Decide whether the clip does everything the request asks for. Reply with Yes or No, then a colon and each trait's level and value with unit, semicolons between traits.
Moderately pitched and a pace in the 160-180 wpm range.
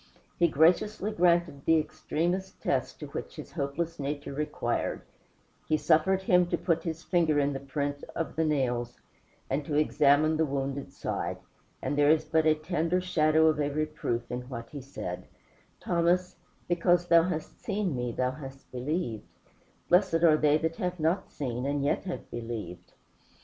Yes: medium, 155 Hz; average, 165 wpm